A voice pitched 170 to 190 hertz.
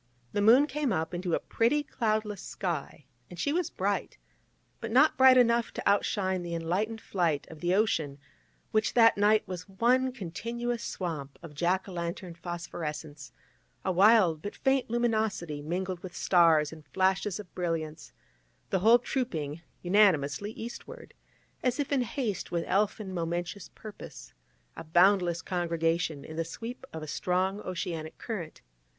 Yes: medium, 185 Hz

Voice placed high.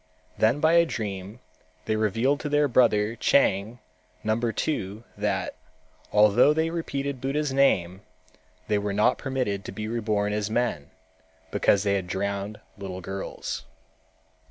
No: low, 110 Hz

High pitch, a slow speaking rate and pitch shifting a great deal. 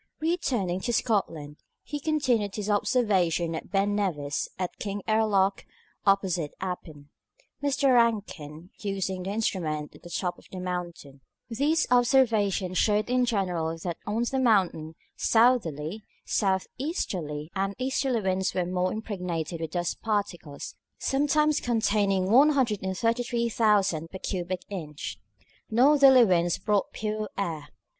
No: high, 200 Hz; slow, 125 wpm; average, 5.0 semitones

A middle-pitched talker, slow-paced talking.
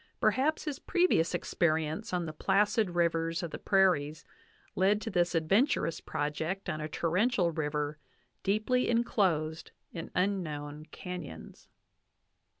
Yes: medium, 175 Hz; slow, 120 wpm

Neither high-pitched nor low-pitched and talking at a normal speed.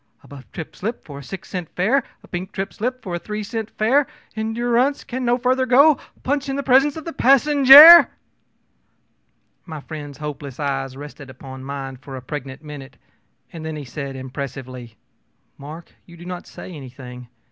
Yes: medium, 170 Hz; average, 180 wpm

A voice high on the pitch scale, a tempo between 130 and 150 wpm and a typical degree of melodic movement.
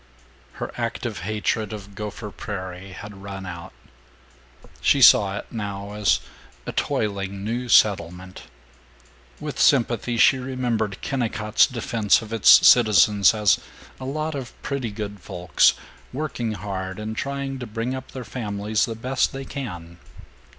No: low, 105 Hz; average, 140 wpm; average, 3.7 semitones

